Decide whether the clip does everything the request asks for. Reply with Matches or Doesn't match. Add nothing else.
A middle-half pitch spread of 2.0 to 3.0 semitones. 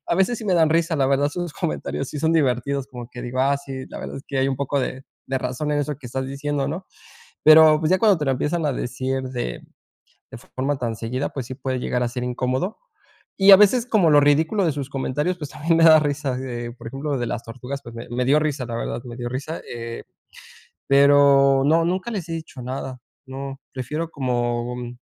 Doesn't match